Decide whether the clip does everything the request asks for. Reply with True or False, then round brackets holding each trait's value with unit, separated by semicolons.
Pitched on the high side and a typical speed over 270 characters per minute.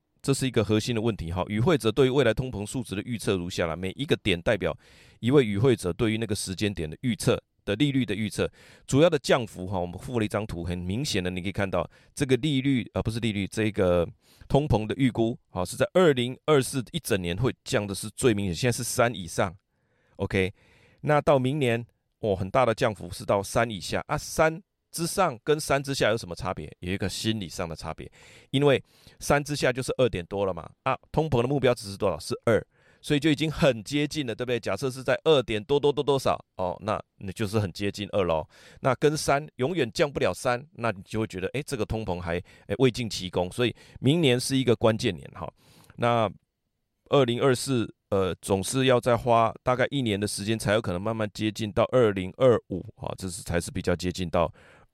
False (115 Hz; 320 characters per minute)